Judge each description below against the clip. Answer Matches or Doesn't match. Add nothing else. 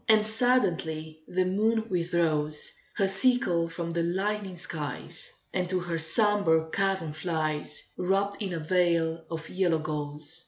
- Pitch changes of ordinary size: Matches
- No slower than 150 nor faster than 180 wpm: Doesn't match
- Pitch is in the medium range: Matches